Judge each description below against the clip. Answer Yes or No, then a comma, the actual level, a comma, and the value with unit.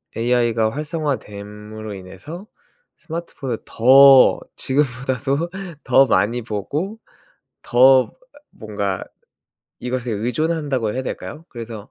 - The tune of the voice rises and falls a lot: No, average, 4.6 semitones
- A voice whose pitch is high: No, low, 125 Hz